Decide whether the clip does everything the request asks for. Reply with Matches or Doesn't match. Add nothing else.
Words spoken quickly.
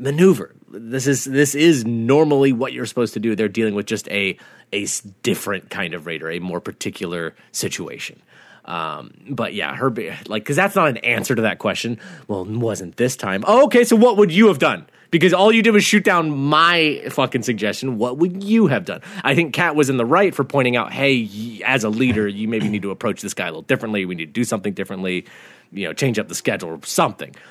Matches